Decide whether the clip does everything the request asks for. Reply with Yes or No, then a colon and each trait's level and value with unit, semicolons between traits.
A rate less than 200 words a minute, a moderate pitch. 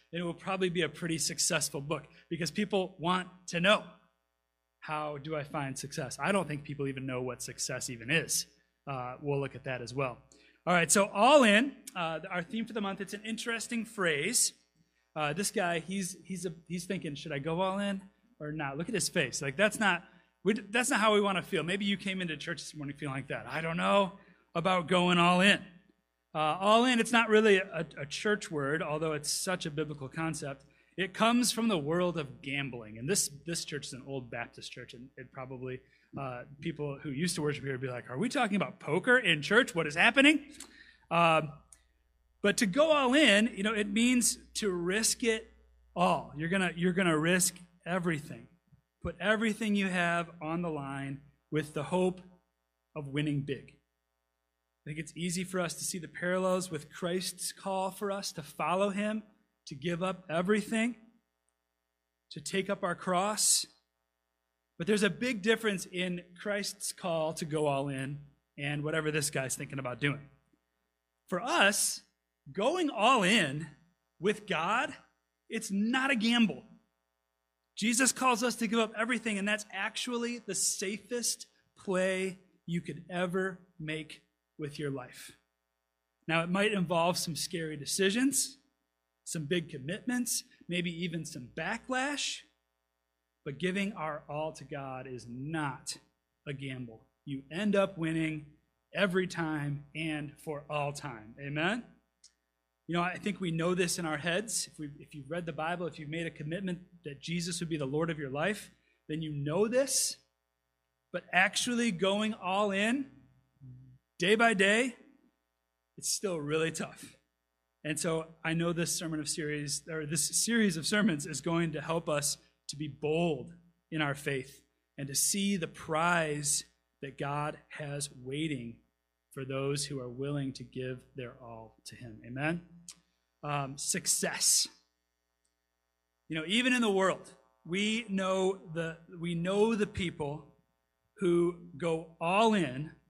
Yes: average, 170 wpm; medium, 165 Hz